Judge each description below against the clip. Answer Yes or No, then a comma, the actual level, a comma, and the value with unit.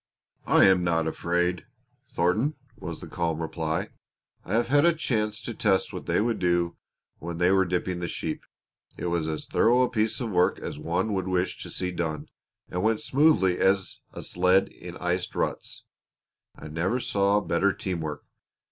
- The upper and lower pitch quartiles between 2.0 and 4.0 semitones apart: Yes, average, 3.6 semitones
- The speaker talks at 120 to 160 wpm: No, average, 180 wpm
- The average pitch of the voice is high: No, very low, 90 Hz